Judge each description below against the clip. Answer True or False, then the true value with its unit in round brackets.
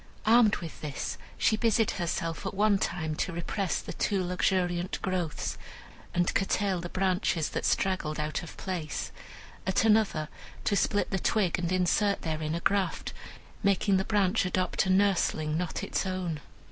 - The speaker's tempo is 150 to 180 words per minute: True (160 wpm)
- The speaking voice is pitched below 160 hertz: False (185 Hz)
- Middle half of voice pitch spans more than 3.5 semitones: False (2.9 semitones)